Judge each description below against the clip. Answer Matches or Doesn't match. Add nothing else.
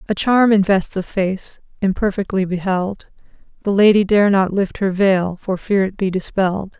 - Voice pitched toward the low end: Doesn't match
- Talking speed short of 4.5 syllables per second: Doesn't match